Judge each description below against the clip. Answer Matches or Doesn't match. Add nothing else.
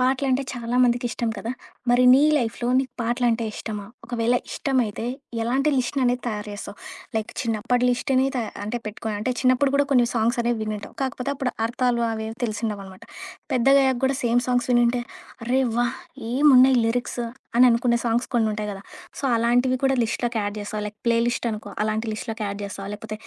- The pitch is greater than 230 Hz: Matches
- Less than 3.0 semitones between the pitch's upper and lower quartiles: Matches